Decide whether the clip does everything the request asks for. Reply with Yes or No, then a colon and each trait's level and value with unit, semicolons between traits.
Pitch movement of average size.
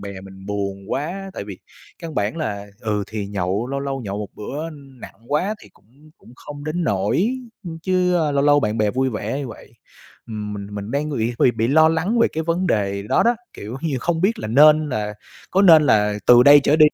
No: wide, 7.1 semitones